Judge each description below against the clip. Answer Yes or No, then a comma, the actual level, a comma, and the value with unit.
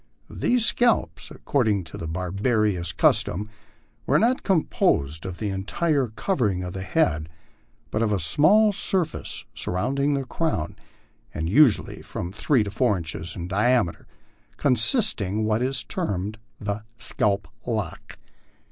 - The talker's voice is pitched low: Yes, low, 105 Hz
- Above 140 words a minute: No, slow, 135 wpm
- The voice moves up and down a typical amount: No, wide, 7.4 semitones